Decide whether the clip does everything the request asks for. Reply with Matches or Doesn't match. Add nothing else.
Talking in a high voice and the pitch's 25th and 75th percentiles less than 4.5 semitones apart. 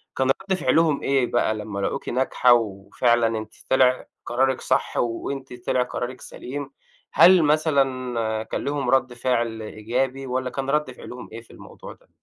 Doesn't match